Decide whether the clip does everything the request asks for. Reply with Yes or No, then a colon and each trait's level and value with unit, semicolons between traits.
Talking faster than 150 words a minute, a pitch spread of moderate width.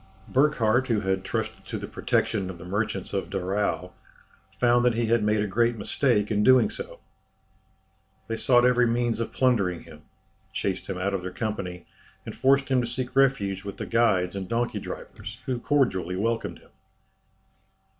Yes: average, 175 wpm; average, 4.1 semitones